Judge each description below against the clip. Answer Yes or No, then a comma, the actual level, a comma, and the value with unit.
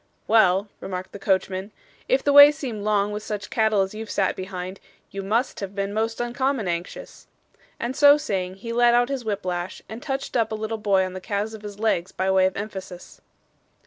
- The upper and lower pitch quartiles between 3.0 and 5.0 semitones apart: Yes, average, 3.4 semitones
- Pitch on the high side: Yes, high, 210 Hz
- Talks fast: Yes, fast, 210 wpm